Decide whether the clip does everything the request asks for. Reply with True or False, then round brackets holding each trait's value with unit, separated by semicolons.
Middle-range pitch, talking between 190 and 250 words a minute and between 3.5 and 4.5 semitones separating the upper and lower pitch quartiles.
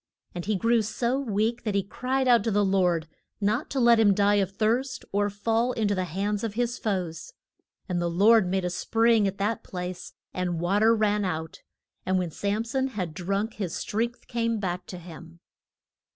False (205 Hz; 200 wpm; 3.9 semitones)